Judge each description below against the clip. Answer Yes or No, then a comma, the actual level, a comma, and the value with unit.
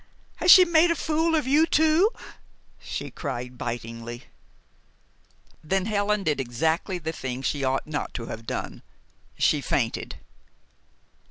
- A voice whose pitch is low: No, medium, 160 Hz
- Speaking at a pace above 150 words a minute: No, slow, 135 wpm